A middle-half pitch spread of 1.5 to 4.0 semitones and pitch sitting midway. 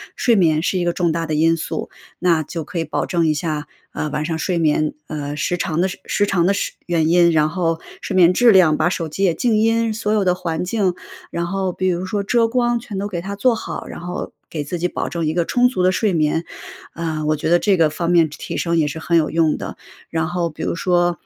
Yes: average, 3.0 semitones; medium, 170 Hz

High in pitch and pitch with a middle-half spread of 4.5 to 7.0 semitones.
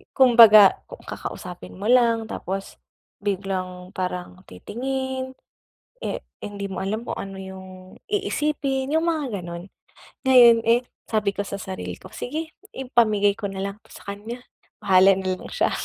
Yes: high, 210 Hz; average, 4.8 semitones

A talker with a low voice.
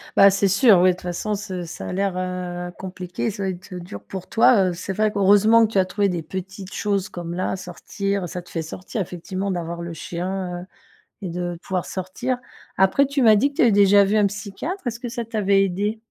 No: high, 190 Hz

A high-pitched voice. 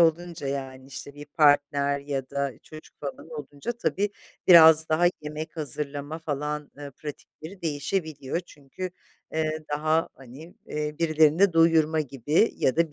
No: medium, 150 Hz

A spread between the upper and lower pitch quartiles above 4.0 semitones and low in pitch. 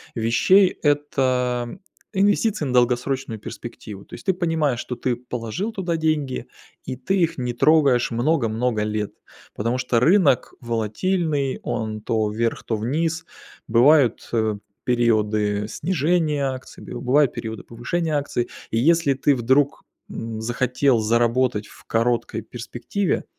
Yes: average, 4.6 semitones; low, 125 Hz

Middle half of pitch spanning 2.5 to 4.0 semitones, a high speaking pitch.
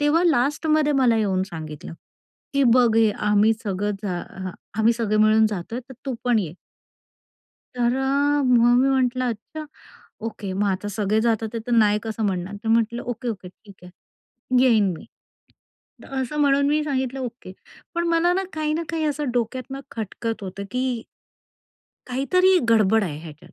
No: average, 4.5 semitones; high, 235 Hz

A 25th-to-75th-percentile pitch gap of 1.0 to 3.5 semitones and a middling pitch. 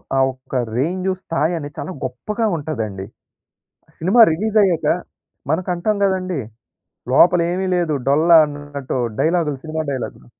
No: average, 4.2 semitones; medium, 160 Hz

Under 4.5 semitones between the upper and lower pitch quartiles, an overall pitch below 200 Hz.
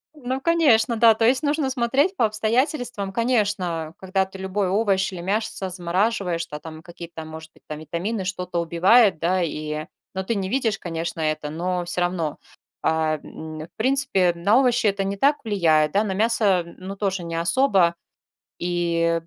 No: average, 4.9 semitones; high, 190 Hz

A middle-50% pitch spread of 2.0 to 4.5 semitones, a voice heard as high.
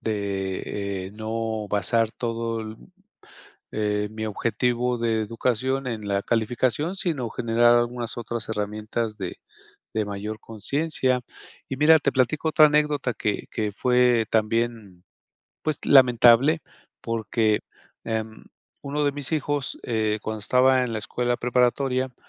No: average, 2.9 semitones; low, 115 Hz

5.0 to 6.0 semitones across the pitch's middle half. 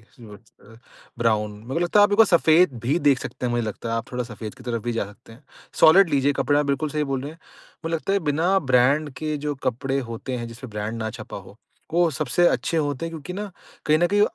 Yes: wide, 5.6 semitones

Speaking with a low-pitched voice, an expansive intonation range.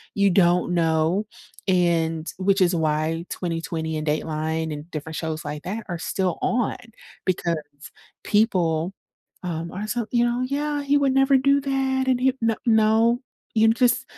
No: medium, 185 Hz; wide, 6.8 semitones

